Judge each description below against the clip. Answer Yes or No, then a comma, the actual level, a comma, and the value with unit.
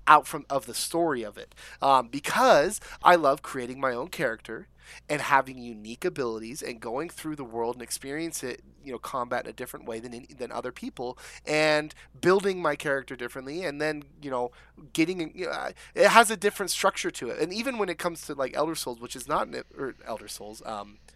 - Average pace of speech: No, fast, 210 wpm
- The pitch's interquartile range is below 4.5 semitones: No, average, 4.9 semitones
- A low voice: No, medium, 145 Hz